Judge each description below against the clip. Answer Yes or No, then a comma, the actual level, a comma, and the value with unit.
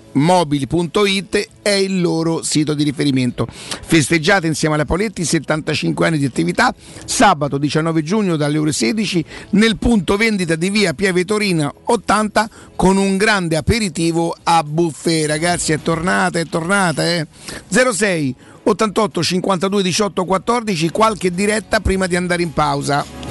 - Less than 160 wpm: Yes, average, 135 wpm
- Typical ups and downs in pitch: Yes, average, 4.4 semitones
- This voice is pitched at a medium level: Yes, medium, 175 Hz